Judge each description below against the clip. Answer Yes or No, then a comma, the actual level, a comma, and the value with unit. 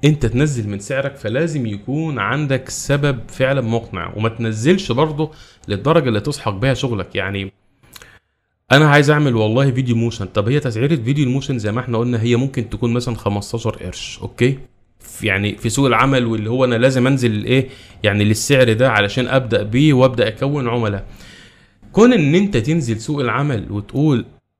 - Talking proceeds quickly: Yes, fast, 165 wpm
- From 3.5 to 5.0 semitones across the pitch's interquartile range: Yes, average, 4.1 semitones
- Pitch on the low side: Yes, low, 125 Hz